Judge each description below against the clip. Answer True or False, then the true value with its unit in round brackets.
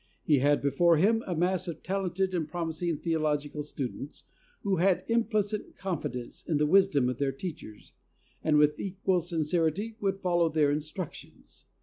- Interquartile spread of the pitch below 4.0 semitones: False (4.3 semitones)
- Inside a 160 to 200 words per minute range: False (150 wpm)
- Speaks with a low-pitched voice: False (165 Hz)